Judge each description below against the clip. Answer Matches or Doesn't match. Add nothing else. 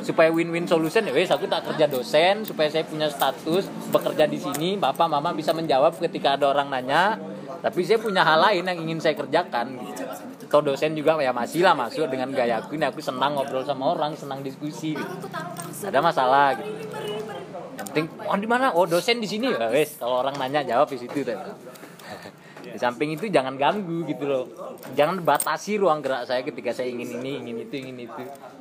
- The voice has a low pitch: Doesn't match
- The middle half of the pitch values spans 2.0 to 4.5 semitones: Matches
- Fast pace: Matches